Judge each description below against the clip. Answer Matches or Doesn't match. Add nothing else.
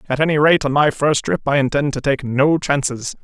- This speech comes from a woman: Doesn't match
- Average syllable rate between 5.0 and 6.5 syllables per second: Matches